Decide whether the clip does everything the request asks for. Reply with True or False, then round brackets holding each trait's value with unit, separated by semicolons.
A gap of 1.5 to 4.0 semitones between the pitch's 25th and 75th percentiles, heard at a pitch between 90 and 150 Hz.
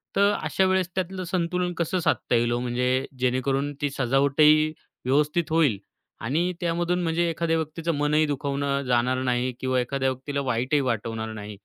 False (4.8 semitones; 140 Hz)